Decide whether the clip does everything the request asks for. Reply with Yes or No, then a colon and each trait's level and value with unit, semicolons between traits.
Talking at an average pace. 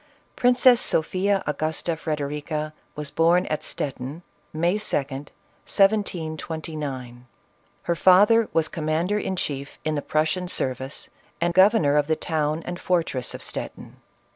No: slow, 130 wpm